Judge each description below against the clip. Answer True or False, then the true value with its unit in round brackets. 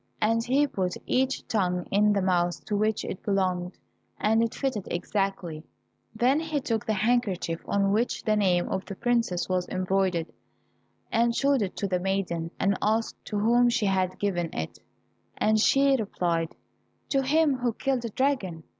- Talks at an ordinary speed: True (170 wpm)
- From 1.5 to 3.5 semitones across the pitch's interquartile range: False (4.4 semitones)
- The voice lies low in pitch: False (205 Hz)